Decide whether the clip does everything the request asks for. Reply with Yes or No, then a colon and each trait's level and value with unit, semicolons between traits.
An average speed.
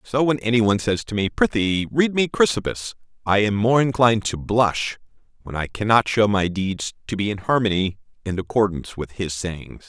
Yes: average, 195 wpm